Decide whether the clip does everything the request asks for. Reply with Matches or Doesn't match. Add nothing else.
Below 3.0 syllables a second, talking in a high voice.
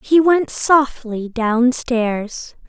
Matches